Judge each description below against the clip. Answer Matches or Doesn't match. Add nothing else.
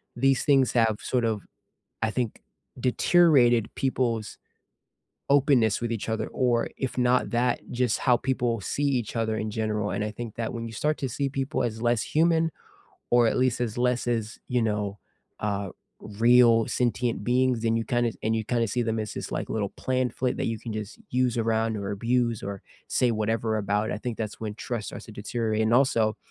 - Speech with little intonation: Matches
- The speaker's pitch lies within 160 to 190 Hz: Doesn't match